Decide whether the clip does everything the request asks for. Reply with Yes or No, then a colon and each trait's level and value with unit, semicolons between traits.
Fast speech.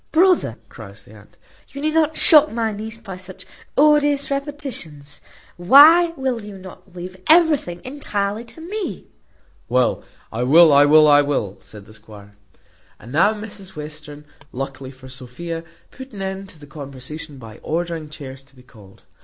No: average, 160 wpm